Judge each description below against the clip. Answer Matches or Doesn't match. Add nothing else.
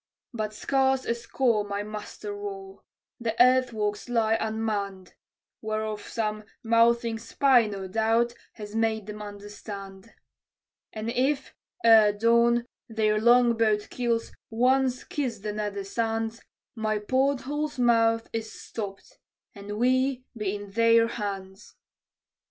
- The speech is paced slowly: Matches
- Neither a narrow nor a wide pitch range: Doesn't match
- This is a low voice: Doesn't match